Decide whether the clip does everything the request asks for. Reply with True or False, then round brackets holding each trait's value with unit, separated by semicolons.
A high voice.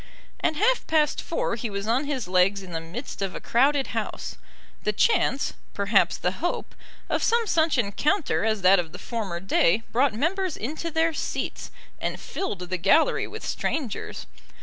True (235 Hz)